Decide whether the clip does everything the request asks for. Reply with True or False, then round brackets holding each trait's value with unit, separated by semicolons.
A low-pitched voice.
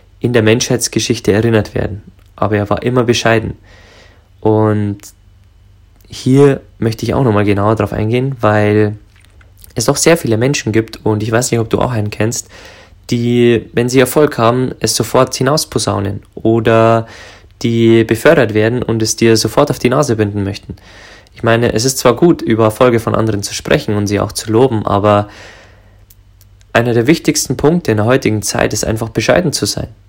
True (110 Hz)